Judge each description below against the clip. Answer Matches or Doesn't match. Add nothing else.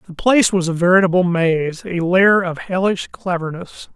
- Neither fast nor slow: Matches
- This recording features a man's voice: Matches